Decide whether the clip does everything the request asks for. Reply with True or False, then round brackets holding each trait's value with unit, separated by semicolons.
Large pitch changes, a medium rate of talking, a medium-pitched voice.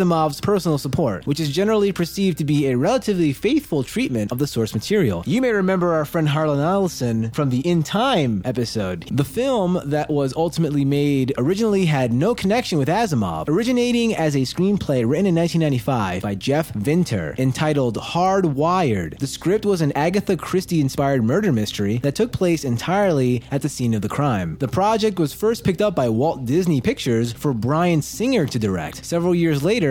True (6.0 semitones; 180 wpm; 150 Hz)